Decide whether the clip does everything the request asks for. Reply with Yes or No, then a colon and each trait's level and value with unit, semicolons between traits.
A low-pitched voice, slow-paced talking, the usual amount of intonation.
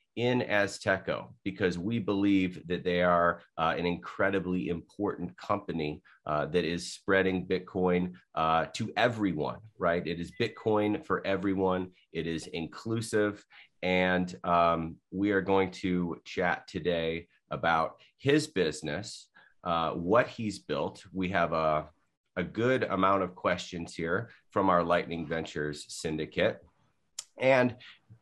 Yes: very low, 90 Hz; slow, 130 wpm; average, 3.1 semitones